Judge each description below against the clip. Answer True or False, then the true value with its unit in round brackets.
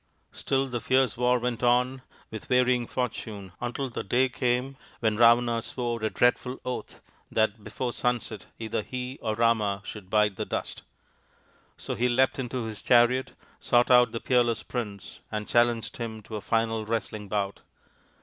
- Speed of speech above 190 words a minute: False (160 wpm)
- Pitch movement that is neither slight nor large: False (2.3 semitones)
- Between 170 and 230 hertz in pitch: False (120 Hz)